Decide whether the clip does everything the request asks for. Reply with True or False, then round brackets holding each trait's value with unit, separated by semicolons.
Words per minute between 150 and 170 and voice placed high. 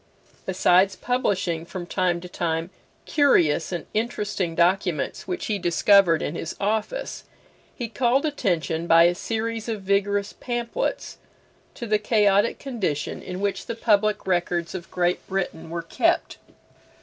False (135 wpm; 195 Hz)